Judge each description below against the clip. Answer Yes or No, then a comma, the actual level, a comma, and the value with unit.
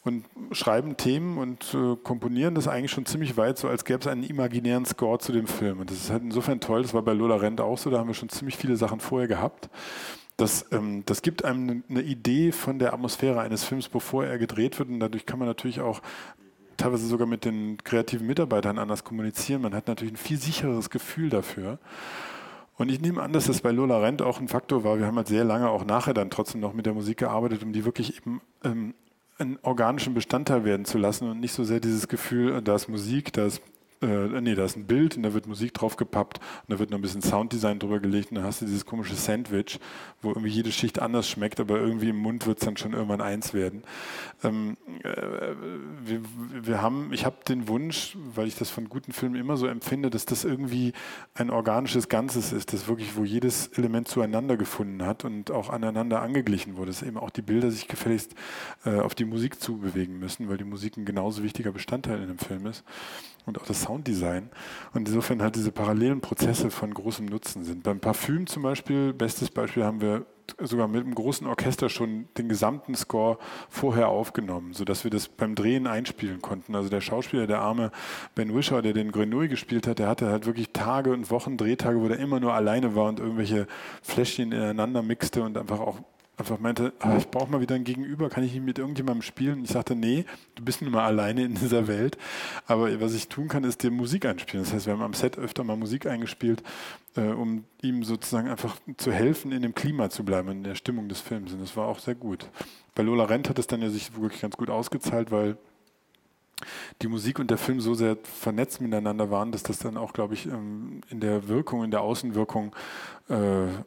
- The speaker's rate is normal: No, fast, 220 wpm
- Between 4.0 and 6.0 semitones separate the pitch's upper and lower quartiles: No, average, 2.9 semitones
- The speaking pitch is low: Yes, low, 115 Hz